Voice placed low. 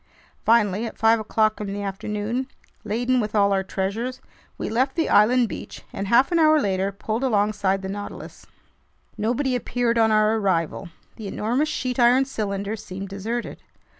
No: high, 215 Hz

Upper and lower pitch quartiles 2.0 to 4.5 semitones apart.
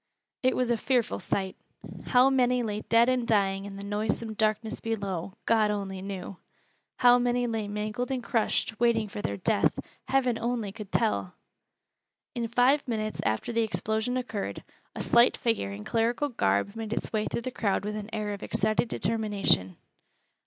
Yes: average, 2.8 semitones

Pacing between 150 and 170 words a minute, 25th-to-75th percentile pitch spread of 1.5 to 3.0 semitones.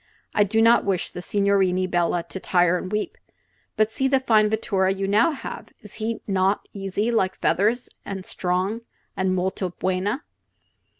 Yes: average, 165 wpm; narrow, 2.6 semitones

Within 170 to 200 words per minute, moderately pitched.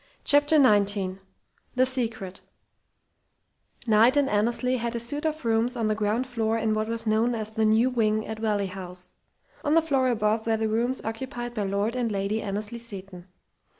No: average, 180 wpm; high, 225 Hz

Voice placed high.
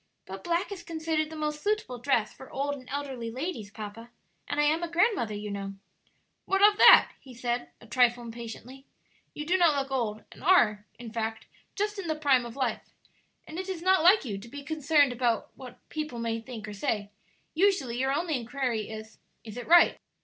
Yes: very high, 265 Hz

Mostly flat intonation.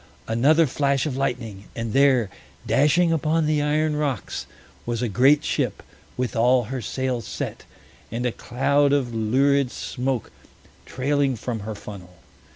No: average, 3.6 semitones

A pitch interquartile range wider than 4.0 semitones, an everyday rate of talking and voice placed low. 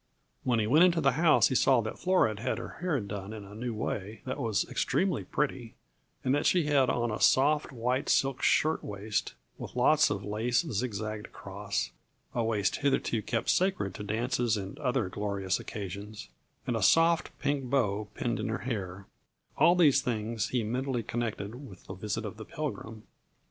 Yes: average, 4.6 semitones; average, 180 wpm; low, 115 Hz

